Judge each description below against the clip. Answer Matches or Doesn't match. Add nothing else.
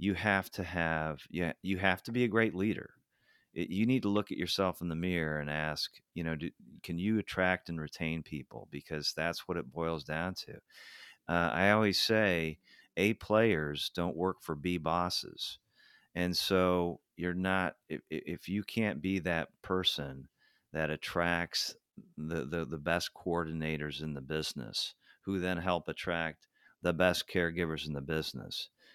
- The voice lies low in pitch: Matches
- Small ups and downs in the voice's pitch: Doesn't match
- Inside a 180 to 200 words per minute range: Doesn't match